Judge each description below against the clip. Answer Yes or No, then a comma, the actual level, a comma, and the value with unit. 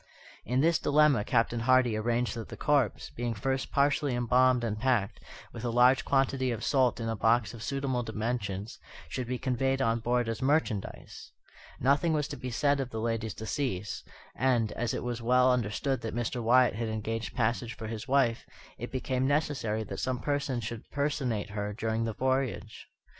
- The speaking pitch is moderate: No, low, 120 Hz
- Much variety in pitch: No, average, 2.8 semitones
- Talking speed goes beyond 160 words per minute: Yes, average, 180 wpm